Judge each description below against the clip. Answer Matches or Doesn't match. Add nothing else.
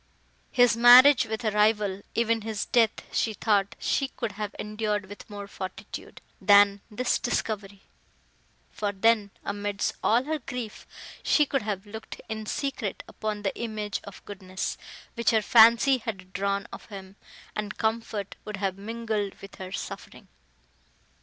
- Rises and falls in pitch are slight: Matches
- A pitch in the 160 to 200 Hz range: Doesn't match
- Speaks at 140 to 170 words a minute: Matches